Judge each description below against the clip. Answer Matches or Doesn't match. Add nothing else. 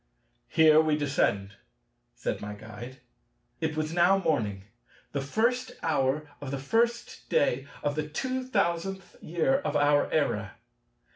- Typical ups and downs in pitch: Doesn't match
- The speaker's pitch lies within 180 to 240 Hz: Doesn't match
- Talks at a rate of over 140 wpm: Doesn't match